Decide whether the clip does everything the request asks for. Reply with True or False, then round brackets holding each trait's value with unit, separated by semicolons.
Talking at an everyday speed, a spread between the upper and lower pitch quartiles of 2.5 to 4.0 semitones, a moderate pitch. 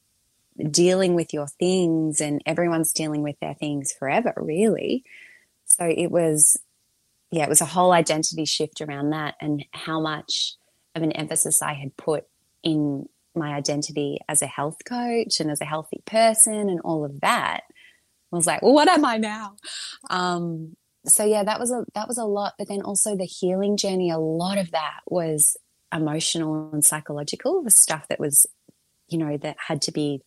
True (180 wpm; 3.7 semitones; 160 Hz)